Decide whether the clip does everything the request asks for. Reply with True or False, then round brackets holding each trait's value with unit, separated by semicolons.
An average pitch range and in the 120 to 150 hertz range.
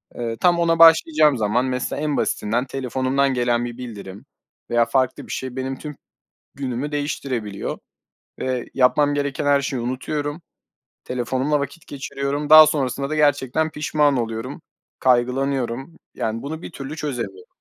True (3.1 semitones; 135 Hz)